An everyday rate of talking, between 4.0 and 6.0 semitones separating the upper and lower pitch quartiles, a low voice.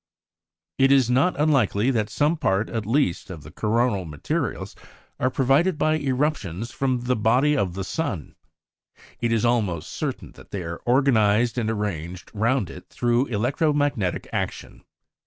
Yes: average, 155 wpm; average, 5.2 semitones; low, 120 Hz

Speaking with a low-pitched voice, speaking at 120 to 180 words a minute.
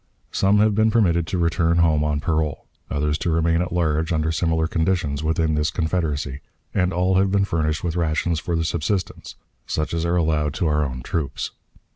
No: very low, 80 Hz; average, 190 wpm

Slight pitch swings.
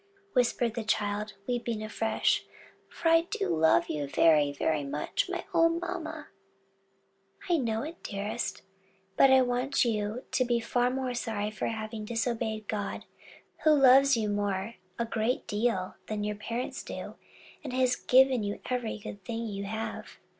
No: average, 3.6 semitones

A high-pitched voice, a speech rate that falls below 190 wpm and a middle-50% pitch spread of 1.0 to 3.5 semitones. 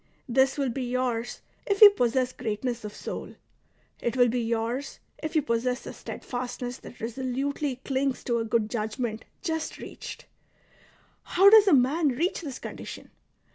Yes: very high, 250 Hz; average, 155 wpm; average, 3.0 semitones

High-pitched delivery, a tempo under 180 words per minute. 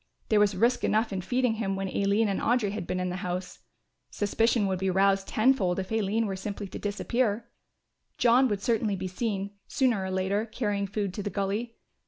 No: high, 205 Hz; average, 200 wpm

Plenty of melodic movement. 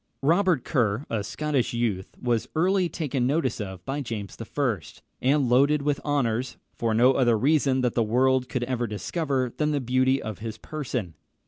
No: average, 3.9 semitones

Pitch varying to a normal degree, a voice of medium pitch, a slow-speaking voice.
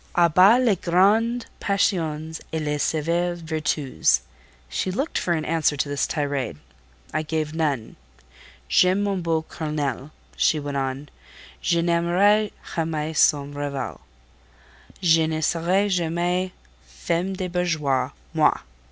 Yes: average, 3.4 semitones; medium, 160 Hz; slow, 125 wpm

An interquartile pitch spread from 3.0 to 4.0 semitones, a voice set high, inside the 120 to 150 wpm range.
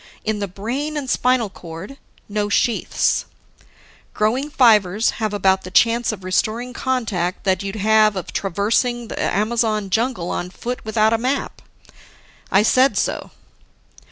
Yes: average, 3.5 semitones; high, 215 Hz; average, 140 wpm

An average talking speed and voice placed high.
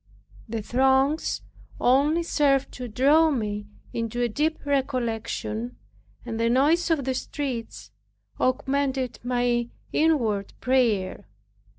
No: slow, 105 wpm; very high, 255 Hz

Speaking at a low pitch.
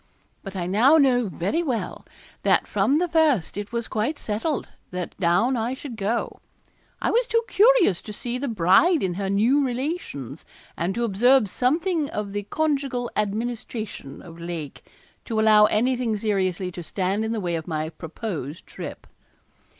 No: high, 220 Hz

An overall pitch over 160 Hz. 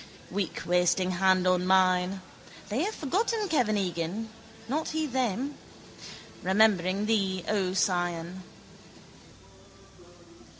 Yes: high, 190 Hz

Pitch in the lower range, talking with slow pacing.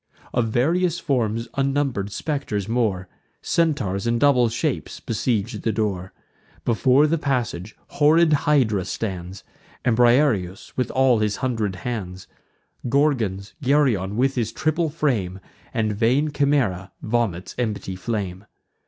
Yes: low, 115 Hz; slow, 120 wpm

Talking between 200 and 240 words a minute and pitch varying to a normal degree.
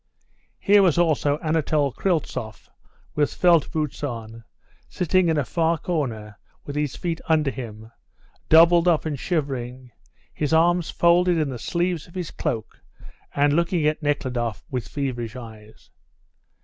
No: average, 140 wpm; average, 5.0 semitones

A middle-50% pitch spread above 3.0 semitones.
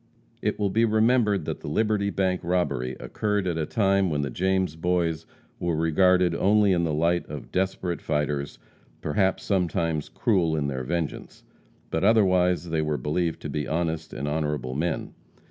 Yes: average, 3.7 semitones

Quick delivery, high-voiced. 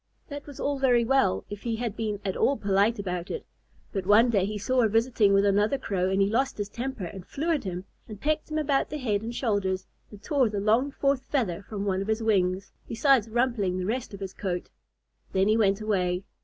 Yes: fast, 230 wpm; high, 215 Hz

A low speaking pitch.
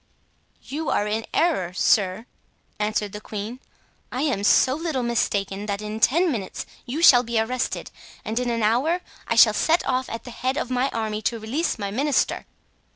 No: high, 235 Hz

